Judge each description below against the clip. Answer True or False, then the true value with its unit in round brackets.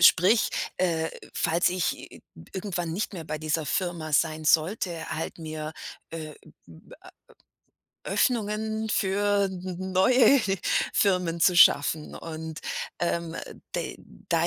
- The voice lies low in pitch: False (175 Hz)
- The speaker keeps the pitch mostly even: False (3.5 semitones)